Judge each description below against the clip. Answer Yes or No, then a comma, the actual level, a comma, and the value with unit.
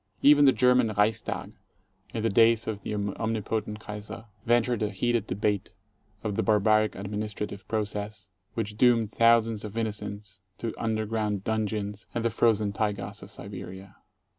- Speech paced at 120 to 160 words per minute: Yes, average, 155 wpm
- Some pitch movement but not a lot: No, narrow, 1.7 semitones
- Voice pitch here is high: No, low, 110 Hz